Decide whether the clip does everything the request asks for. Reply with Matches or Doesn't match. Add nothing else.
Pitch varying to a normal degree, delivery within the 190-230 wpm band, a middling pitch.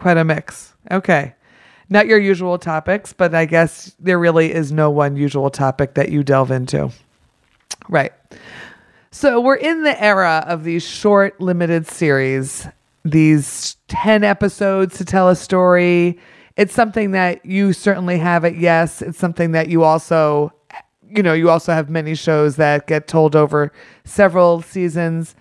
Doesn't match